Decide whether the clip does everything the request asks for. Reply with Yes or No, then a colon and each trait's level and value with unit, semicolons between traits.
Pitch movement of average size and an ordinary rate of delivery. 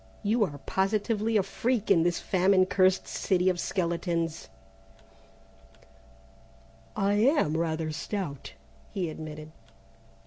No: average, 3.7 semitones; slow, 105 wpm